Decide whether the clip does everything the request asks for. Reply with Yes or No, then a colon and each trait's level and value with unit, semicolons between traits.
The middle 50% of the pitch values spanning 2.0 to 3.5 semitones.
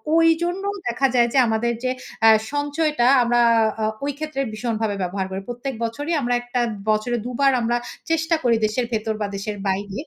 No: average, 4.5 semitones